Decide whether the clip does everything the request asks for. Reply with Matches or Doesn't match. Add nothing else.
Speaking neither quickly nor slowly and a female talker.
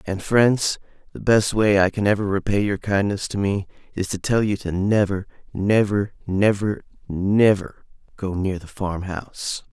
Doesn't match